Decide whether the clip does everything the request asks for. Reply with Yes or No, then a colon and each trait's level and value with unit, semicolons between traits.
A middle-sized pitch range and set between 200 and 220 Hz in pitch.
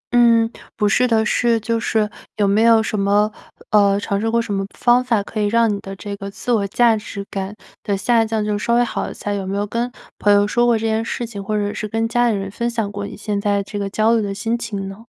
No: narrow, 2.3 semitones; high, 215 Hz